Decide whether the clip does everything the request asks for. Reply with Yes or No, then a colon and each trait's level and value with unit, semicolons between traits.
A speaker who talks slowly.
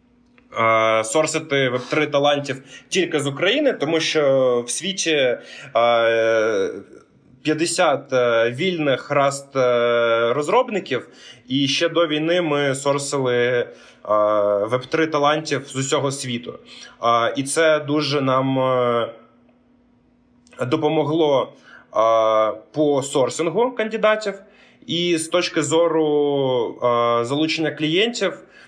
Yes: slow, 85 wpm